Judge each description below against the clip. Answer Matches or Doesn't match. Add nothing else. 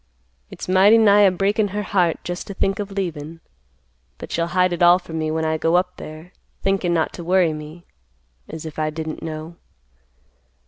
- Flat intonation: Doesn't match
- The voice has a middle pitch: Matches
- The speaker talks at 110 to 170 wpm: Doesn't match